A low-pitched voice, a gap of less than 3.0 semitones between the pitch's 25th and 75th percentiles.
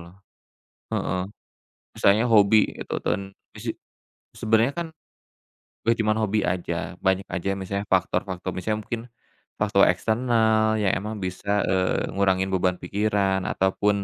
Yes: low, 100 Hz; narrow, 2.5 semitones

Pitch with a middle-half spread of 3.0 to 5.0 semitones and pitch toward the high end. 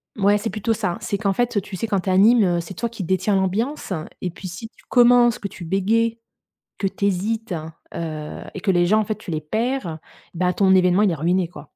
Yes: average, 3.7 semitones; high, 195 Hz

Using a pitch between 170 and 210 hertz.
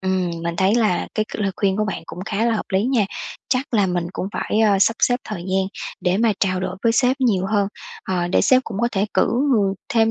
Yes: high, 205 Hz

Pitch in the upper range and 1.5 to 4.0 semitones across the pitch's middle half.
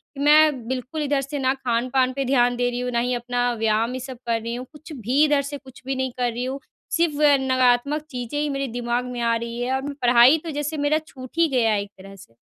Yes: very high, 255 Hz; narrow, 2.5 semitones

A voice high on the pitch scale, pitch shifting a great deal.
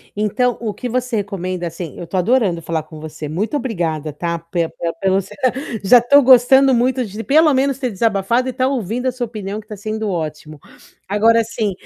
Yes: high, 215 Hz; wide, 6.2 semitones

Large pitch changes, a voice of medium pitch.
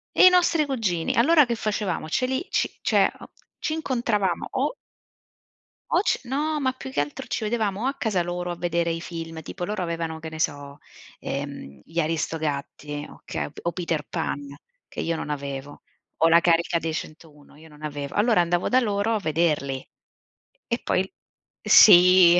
Yes: wide, 6.0 semitones; medium, 170 Hz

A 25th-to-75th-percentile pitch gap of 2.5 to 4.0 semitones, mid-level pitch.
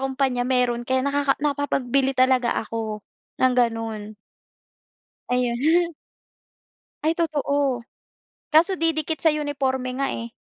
No: average, 2.9 semitones; very high, 265 Hz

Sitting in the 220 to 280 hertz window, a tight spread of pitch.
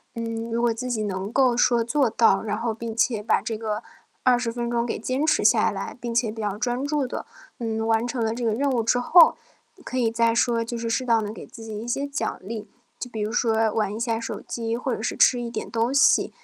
Yes: high, 230 Hz; narrow, 1.6 semitones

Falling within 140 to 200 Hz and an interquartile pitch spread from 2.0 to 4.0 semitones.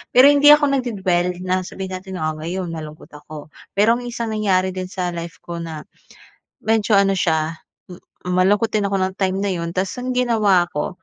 Yes: high, 190 Hz; average, 3.7 semitones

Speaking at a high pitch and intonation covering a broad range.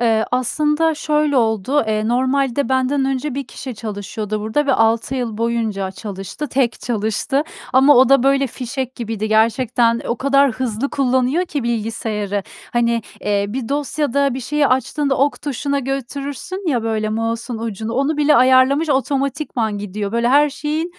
No: very high, 255 Hz; average, 3.8 semitones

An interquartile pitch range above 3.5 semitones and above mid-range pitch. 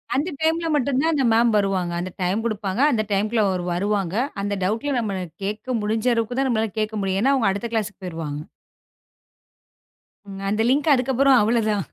Yes: average, 4.3 semitones; high, 215 Hz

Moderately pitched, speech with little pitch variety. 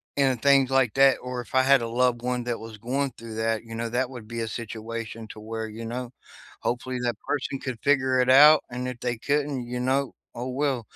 No: low, 125 Hz; narrow, 2.3 semitones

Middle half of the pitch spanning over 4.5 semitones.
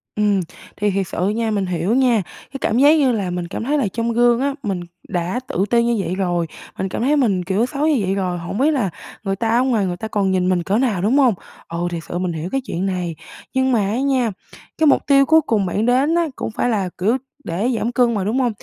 Yes: wide, 5.4 semitones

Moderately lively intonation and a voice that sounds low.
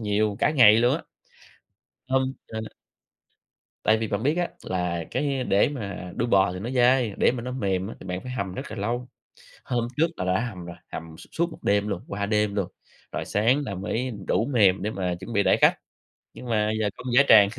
Yes: average, 4.0 semitones; low, 105 Hz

